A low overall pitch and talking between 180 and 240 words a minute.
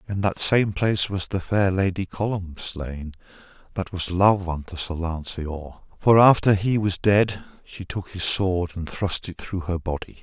Yes: very low, 95 Hz; average, 190 wpm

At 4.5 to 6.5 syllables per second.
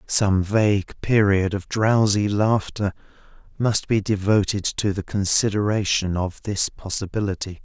No: 4.2 syllables/s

